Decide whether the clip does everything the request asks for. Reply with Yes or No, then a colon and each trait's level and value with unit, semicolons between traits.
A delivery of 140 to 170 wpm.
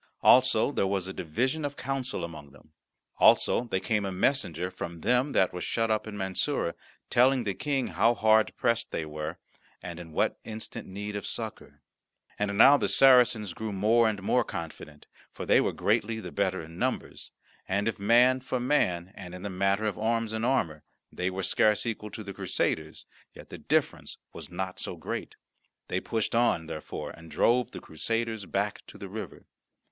No: average, 185 wpm